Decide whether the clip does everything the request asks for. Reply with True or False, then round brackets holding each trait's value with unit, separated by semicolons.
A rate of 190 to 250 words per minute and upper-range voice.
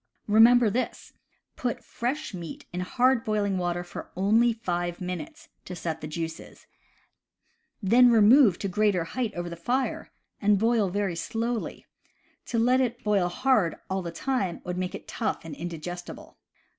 False (155 wpm; 205 Hz)